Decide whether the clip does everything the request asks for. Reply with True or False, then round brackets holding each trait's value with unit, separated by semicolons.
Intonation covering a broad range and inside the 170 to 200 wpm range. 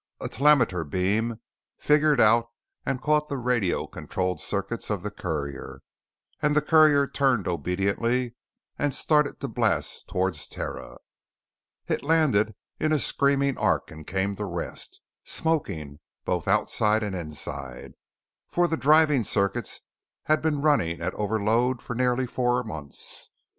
False (7.0 semitones; 135 wpm)